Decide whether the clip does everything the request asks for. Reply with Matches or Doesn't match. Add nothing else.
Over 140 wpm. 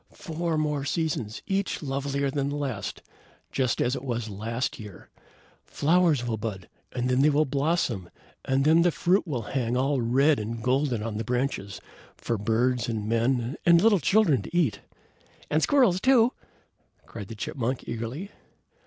Matches